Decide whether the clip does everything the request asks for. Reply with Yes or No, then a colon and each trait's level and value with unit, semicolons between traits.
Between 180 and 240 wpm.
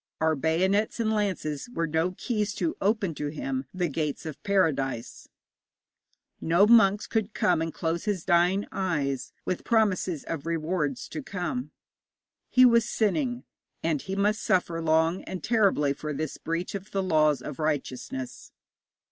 No: average, 150 wpm